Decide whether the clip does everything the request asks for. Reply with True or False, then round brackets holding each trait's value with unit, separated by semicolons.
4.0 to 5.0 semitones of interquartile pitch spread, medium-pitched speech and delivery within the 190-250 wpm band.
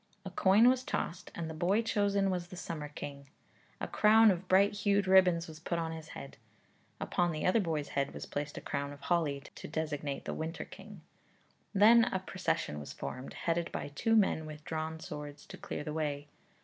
True (4.7 semitones; 165 Hz; 200 wpm)